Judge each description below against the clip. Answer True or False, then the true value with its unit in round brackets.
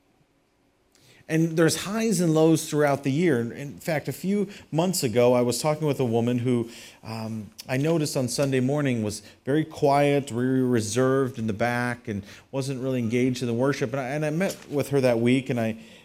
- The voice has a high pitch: False (135 Hz)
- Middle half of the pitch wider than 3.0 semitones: True (3.7 semitones)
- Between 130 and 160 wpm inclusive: False (200 wpm)